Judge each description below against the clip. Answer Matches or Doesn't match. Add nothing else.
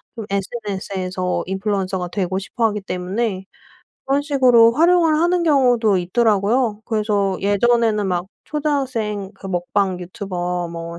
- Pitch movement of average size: Matches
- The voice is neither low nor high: Doesn't match